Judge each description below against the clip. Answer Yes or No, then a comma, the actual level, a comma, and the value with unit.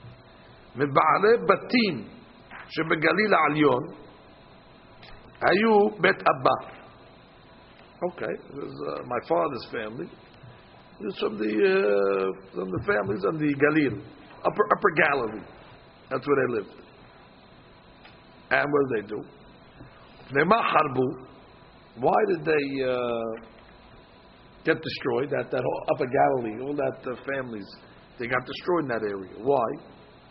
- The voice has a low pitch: Yes, low, 130 Hz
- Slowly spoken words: Yes, slow, 100 wpm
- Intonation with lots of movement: Yes, wide, 6.0 semitones